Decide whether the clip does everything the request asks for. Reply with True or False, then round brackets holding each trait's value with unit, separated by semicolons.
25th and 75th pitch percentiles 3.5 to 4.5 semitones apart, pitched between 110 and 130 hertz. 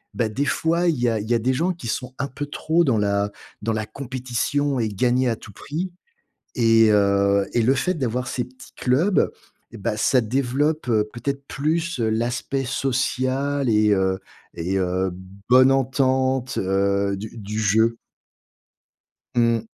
True (4.0 semitones; 125 Hz)